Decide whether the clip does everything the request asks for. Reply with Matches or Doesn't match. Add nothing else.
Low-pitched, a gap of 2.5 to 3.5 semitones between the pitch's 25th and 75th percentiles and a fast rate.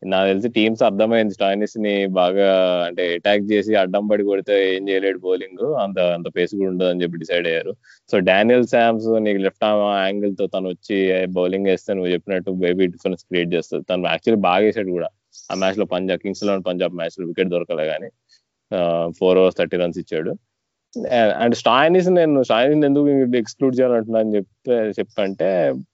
Matches